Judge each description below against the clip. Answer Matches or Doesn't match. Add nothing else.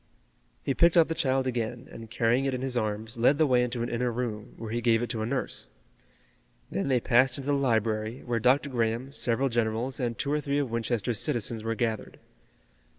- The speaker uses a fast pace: Matches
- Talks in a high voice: Doesn't match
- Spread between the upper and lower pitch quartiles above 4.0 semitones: Doesn't match